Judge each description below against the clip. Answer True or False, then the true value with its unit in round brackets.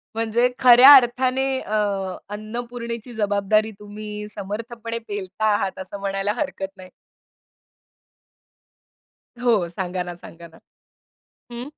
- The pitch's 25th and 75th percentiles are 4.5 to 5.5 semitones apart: False (3.3 semitones)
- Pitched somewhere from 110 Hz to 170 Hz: False (215 Hz)